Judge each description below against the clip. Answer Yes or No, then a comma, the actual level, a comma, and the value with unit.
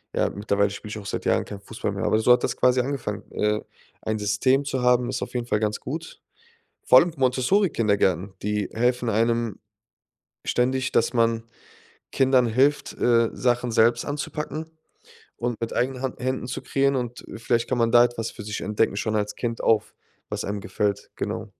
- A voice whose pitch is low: Yes, low, 120 Hz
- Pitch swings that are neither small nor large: Yes, average, 3.2 semitones